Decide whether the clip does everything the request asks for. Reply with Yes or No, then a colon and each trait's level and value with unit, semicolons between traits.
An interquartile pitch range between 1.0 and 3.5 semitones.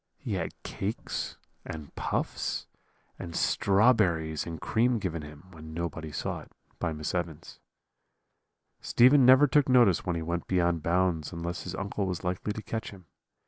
No: average, 4.5 semitones